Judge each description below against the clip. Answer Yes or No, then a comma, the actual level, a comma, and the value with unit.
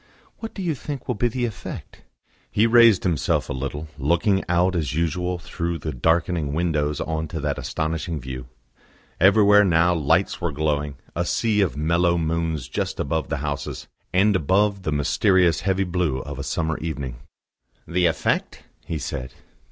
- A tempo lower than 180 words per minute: Yes, average, 165 wpm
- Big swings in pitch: No, average, 3.8 semitones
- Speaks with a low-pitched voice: Yes, very low, 85 Hz